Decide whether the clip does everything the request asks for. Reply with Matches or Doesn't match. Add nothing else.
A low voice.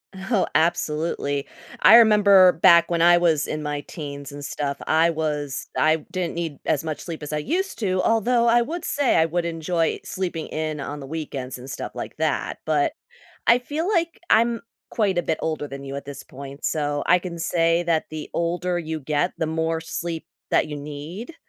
Doesn't match